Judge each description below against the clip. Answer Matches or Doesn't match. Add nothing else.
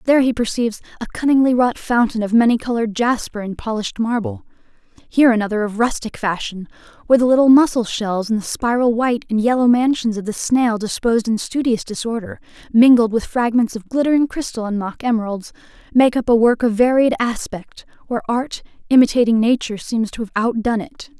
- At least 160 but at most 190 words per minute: Matches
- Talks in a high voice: Matches